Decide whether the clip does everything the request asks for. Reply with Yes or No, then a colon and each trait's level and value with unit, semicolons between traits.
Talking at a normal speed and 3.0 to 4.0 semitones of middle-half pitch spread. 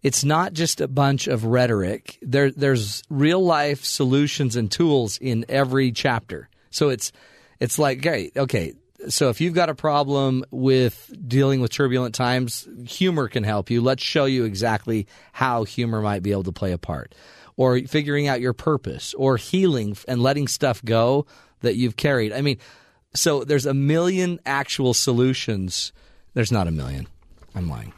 Yes: average, 170 wpm; average, 3.3 semitones